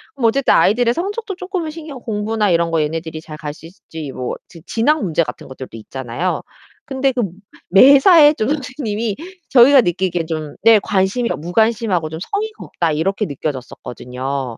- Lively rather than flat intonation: Yes, wide, 8.8 semitones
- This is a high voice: Yes, high, 200 Hz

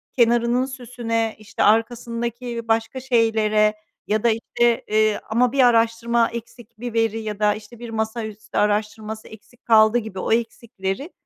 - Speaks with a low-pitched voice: No, high, 225 Hz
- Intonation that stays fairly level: Yes, narrow, 1.6 semitones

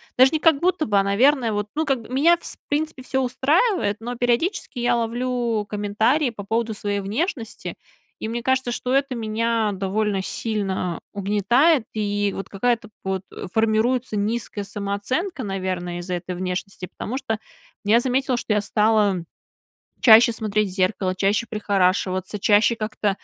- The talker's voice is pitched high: Yes, high, 220 Hz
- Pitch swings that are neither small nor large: Yes, average, 3.8 semitones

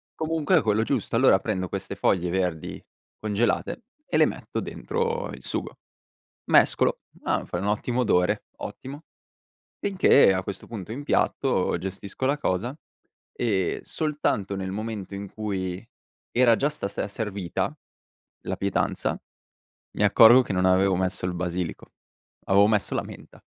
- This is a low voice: Yes, low, 105 Hz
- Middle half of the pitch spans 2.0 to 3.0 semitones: No, average, 5.1 semitones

